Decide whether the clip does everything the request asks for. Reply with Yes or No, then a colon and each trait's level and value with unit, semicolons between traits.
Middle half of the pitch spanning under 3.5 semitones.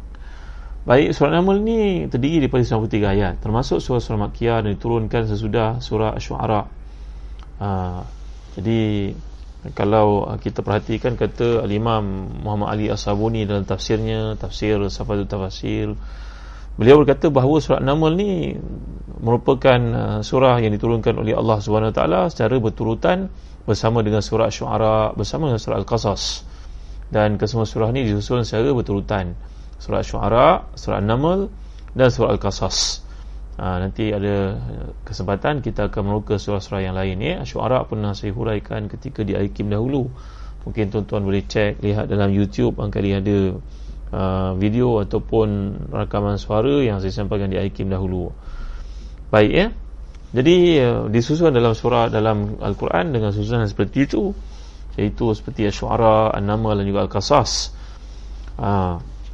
Yes: average, 2.8 semitones